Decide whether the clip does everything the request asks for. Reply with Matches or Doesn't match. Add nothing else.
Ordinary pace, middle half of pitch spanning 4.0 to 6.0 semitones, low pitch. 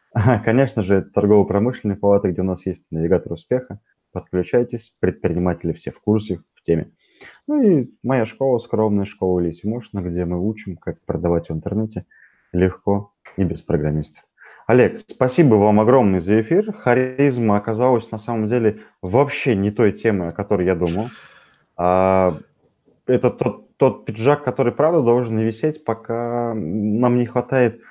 Matches